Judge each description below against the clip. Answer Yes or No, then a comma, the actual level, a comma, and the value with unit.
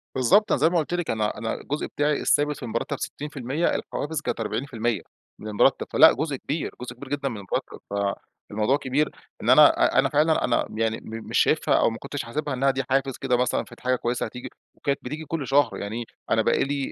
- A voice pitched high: No, low, 135 Hz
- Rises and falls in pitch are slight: No, average, 3.7 semitones